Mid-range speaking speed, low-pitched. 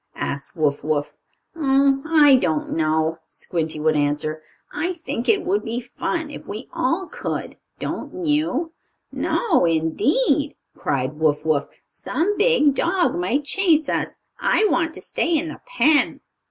No: average, 145 wpm; very high, 270 Hz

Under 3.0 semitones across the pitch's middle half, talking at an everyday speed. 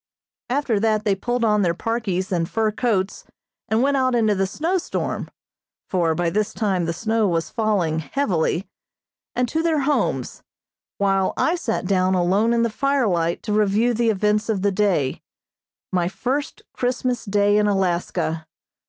No: average, 4.2 semitones; average, 160 wpm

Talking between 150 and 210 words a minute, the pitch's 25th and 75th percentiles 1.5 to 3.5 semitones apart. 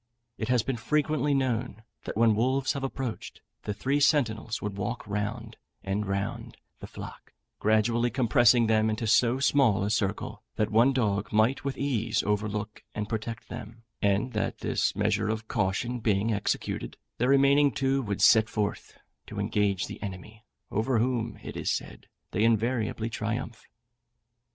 Yes: average, 155 wpm; average, 3.0 semitones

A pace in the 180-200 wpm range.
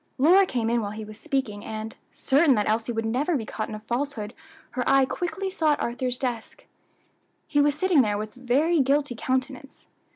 Yes: average, 195 wpm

